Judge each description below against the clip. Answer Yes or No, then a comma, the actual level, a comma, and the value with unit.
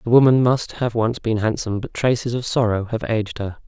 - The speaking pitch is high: No, low, 115 Hz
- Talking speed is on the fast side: Yes, fast, 230 wpm